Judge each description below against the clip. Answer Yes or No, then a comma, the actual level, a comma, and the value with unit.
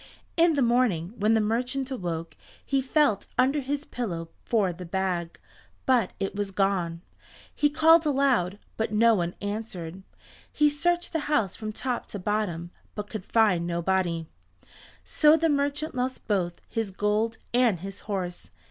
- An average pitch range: No, wide, 6.3 semitones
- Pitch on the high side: Yes, high, 215 Hz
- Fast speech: No, average, 155 wpm